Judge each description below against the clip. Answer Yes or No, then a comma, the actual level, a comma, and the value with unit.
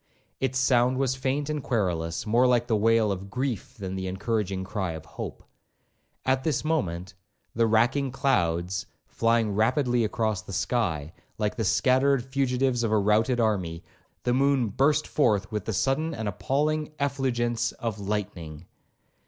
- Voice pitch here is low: Yes, low, 115 Hz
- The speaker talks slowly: No, average, 155 wpm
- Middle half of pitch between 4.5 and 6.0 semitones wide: Yes, average, 4.9 semitones